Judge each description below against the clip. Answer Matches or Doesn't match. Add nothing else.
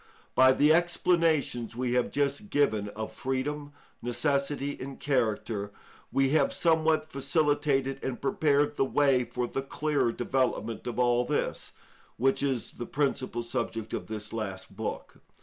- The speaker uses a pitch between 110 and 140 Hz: Matches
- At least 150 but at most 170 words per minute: Doesn't match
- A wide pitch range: Doesn't match